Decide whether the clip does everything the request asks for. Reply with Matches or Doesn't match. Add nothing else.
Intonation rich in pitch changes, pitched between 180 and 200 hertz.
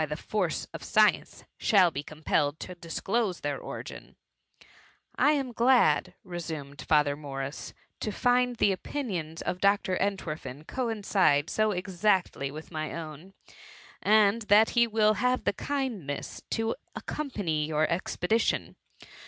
Matches